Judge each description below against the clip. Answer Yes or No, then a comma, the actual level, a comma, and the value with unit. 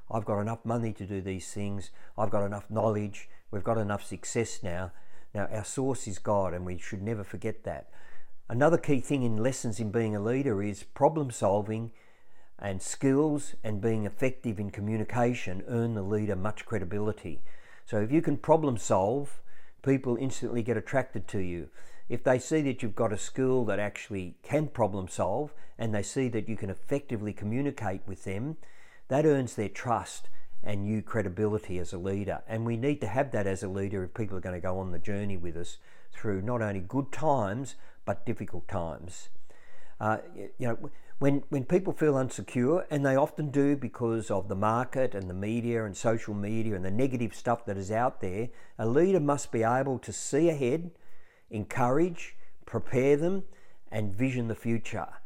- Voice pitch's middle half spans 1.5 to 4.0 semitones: No, average, 4.6 semitones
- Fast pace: No, average, 185 wpm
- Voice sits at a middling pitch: No, low, 110 Hz